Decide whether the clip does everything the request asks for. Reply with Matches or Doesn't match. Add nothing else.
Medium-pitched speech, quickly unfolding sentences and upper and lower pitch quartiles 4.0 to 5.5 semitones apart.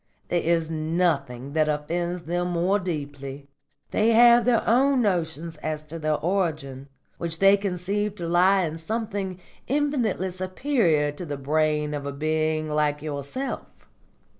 Doesn't match